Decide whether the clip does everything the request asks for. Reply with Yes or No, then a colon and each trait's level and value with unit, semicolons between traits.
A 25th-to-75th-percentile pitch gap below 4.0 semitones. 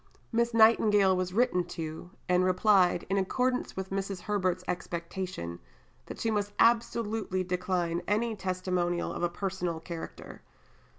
Yes: average, 2.9 semitones